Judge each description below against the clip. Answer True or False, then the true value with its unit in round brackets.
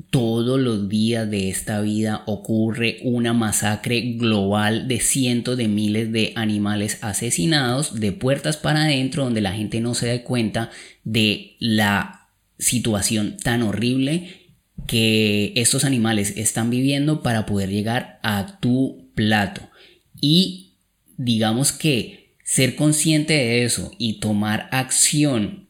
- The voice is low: True (115 Hz)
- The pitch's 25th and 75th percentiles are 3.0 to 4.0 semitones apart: True (3.6 semitones)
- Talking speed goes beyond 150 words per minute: False (125 wpm)